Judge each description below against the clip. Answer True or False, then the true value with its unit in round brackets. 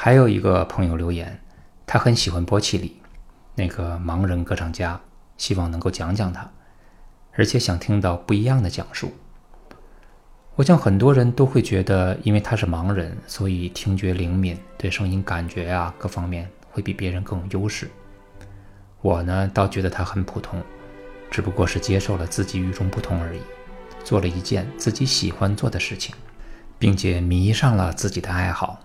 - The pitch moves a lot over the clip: False (2.5 semitones)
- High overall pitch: False (95 Hz)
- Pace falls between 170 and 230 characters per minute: False (260 characters per minute)